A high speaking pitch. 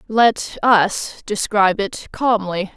Yes: high, 205 Hz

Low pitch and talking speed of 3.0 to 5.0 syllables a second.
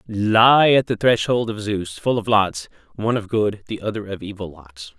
Yes: low, 105 Hz; 4.7 syllables/s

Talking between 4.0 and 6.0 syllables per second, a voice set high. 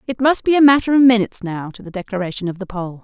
No: 7.0 syllables/s; high, 215 Hz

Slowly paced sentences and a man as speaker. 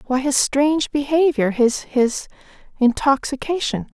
No: slow, 75 wpm; female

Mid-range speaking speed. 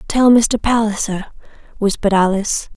No: slow, 110 wpm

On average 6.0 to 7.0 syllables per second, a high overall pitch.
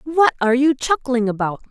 No: 5.5 syllables/s; very high, 260 Hz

